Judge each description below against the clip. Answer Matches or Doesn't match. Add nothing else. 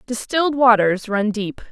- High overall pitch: Matches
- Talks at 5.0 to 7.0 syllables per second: Doesn't match